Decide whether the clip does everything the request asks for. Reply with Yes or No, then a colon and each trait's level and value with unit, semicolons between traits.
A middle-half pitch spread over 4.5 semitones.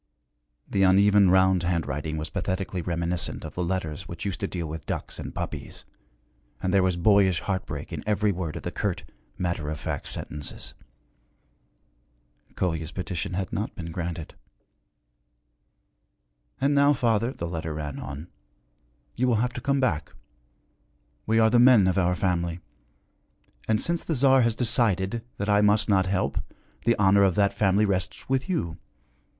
No: average, 3.9 semitones